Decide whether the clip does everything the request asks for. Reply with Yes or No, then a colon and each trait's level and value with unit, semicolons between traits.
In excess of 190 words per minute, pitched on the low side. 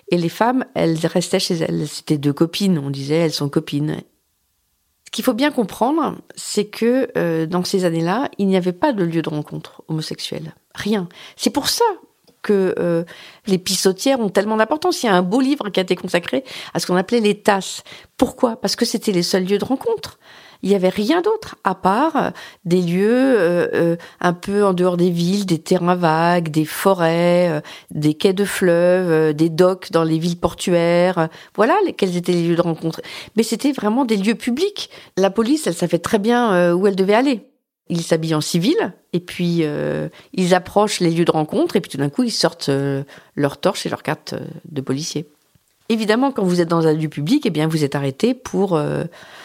No: average, 210 wpm; medium, 180 Hz